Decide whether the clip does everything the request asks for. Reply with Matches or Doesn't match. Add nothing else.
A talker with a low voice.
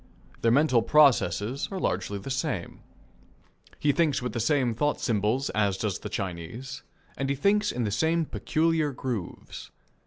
Matches